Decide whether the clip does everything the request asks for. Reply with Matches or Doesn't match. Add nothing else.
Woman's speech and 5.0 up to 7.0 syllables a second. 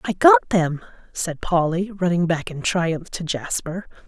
Doesn't match